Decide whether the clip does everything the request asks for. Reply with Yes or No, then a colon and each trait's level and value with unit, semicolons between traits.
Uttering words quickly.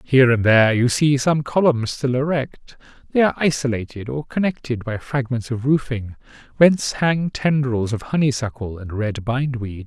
No: average, 165 wpm